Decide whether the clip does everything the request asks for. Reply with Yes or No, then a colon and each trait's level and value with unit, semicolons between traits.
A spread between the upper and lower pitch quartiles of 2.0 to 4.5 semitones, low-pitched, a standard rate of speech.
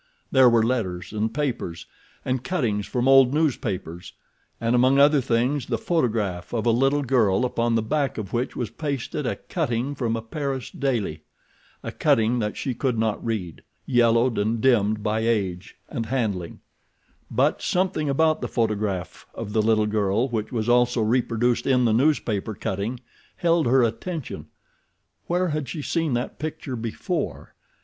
Yes: average, 3.7 semitones; low, 120 Hz; average, 155 wpm